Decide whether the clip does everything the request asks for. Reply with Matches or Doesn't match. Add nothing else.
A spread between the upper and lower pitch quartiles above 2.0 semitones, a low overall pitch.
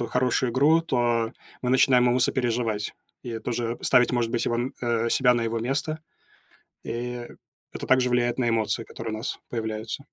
Doesn't match